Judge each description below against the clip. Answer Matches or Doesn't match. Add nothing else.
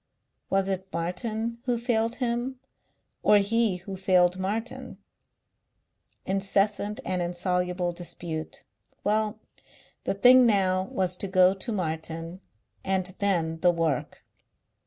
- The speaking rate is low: Matches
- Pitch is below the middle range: Doesn't match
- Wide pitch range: Doesn't match